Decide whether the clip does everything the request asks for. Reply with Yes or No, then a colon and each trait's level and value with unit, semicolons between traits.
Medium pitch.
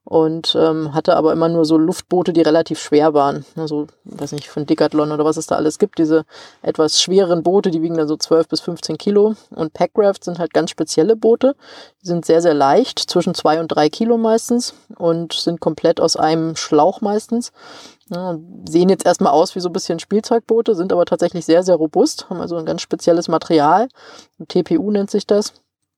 Yes: medium, 170 Hz